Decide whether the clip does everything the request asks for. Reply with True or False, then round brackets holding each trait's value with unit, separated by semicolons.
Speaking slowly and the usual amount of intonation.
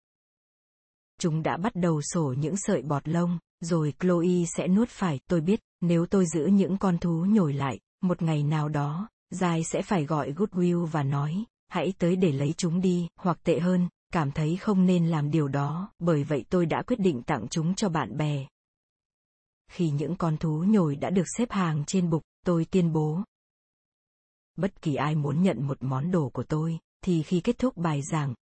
False (195 wpm; 3.2 semitones)